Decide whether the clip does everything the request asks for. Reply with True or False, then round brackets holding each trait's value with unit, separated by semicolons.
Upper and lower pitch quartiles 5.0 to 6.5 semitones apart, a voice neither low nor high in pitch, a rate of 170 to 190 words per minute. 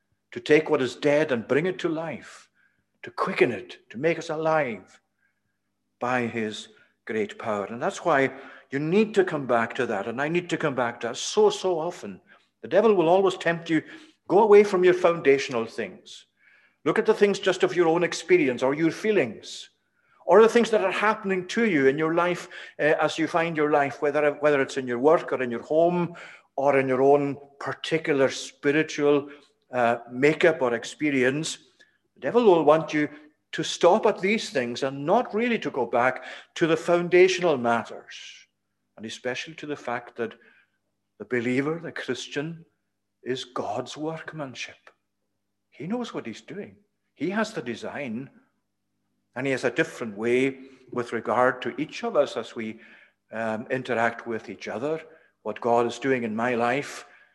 True (5.5 semitones; 150 Hz; 180 wpm)